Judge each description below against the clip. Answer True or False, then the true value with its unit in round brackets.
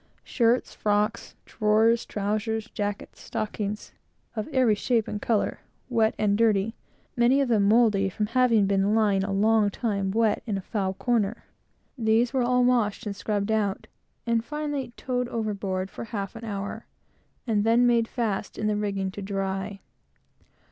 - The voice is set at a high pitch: True (215 Hz)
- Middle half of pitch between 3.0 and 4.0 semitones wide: False (2.5 semitones)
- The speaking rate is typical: True (155 wpm)